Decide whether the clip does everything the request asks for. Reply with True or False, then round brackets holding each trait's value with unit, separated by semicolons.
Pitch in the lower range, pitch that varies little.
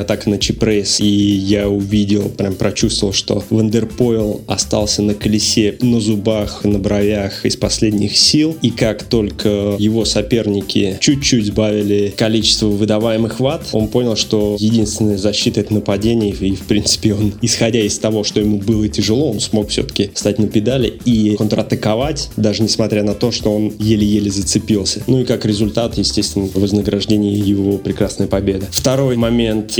True (105 Hz; 1.5 semitones)